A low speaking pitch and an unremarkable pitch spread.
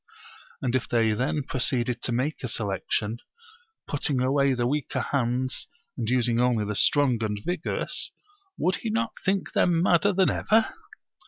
Yes: low, 130 Hz; average, 4.4 semitones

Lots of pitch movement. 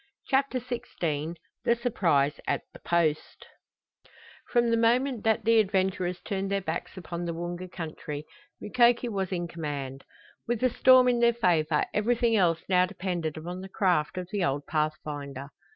Yes: wide, 6.2 semitones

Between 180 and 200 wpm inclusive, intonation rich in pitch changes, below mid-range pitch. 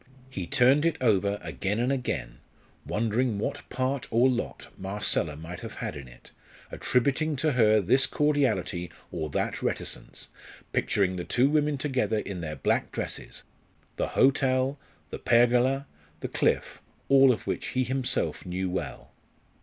No: average, 145 wpm; wide, 6.2 semitones; low, 120 Hz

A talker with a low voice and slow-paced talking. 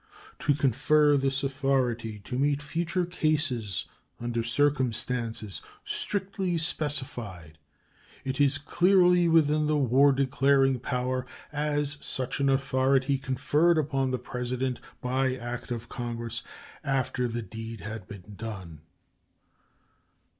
Yes: low, 130 Hz; slow, 110 wpm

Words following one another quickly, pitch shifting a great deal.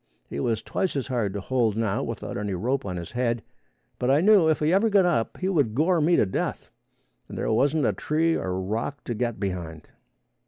Yes: fast, 220 wpm; wide, 7.3 semitones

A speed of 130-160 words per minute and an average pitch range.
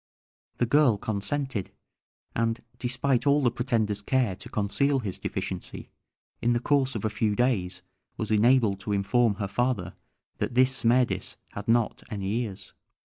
Yes: average, 150 wpm; average, 3.9 semitones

